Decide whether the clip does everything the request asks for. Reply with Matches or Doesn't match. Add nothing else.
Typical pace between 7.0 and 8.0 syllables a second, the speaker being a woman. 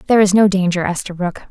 Matches